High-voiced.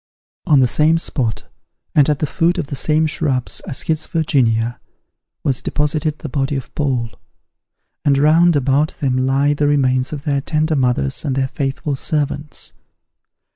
No: medium, 145 Hz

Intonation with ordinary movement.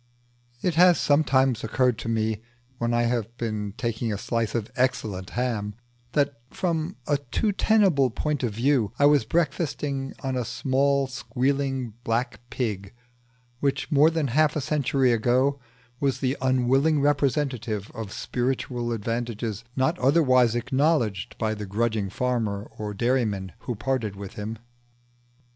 Yes: average, 3.9 semitones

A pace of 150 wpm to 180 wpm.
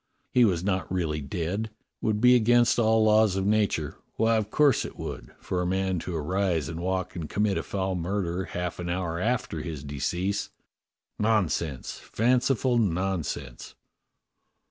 Yes: average, 165 wpm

